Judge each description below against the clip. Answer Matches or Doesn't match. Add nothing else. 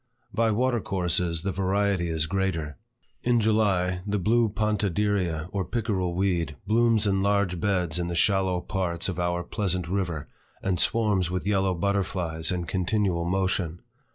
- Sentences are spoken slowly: Doesn't match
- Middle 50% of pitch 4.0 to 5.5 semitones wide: Doesn't match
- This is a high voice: Doesn't match